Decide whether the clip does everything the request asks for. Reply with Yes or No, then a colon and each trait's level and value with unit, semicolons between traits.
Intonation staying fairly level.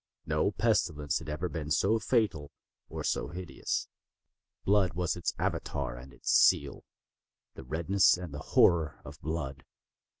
No: average, 3.8 semitones